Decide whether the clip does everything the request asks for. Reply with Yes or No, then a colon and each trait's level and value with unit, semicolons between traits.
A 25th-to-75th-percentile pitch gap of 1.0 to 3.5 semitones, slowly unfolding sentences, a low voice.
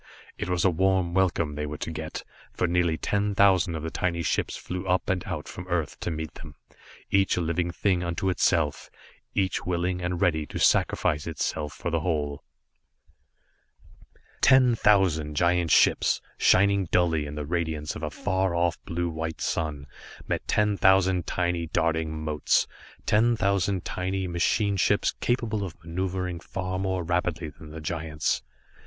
No: average, 2.8 semitones; average, 160 wpm; very low, 85 Hz